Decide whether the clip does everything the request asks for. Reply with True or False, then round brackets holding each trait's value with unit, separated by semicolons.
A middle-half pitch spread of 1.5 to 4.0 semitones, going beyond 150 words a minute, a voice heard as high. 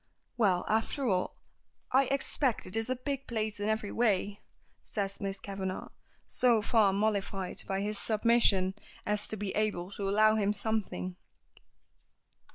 False (2.4 semitones; 145 wpm; 210 Hz)